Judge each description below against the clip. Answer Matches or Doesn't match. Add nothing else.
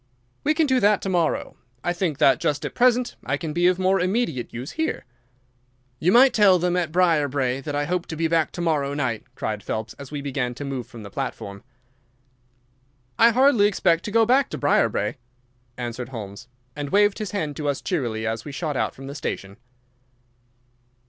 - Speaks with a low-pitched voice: Doesn't match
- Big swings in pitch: Matches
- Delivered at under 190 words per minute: Doesn't match